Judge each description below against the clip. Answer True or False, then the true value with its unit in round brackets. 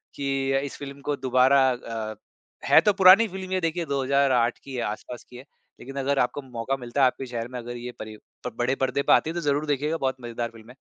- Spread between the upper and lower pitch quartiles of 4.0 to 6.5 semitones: False (2.6 semitones)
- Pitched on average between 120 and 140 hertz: True (135 Hz)